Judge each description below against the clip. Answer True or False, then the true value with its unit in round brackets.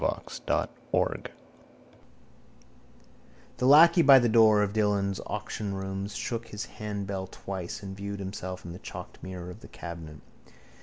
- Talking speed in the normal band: False (130 wpm)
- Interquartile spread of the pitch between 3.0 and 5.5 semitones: False (2.4 semitones)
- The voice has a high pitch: False (100 Hz)